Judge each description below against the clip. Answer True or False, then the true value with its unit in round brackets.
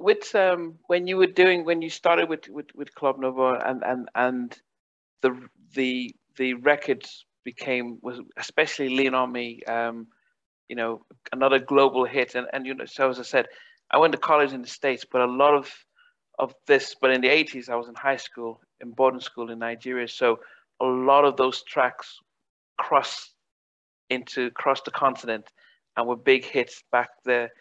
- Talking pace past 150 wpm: True (185 wpm)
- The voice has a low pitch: True (130 Hz)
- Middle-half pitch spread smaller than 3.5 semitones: True (2.9 semitones)